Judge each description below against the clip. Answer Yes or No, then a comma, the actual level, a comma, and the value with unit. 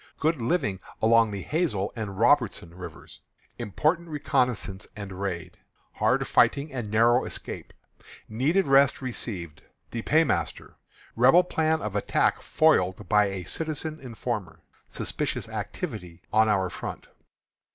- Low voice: Yes, low, 115 Hz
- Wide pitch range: Yes, wide, 6.9 semitones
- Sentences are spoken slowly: Yes, slow, 120 wpm